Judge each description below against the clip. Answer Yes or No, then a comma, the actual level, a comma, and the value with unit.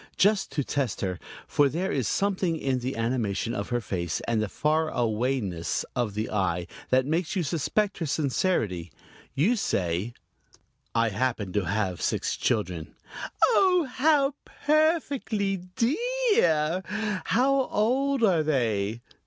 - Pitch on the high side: No, medium, 140 Hz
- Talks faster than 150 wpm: No, slow, 135 wpm